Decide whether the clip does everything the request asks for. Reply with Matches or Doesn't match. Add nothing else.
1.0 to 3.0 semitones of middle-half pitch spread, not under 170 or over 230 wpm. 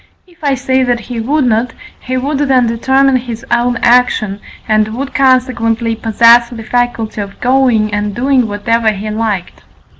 Doesn't match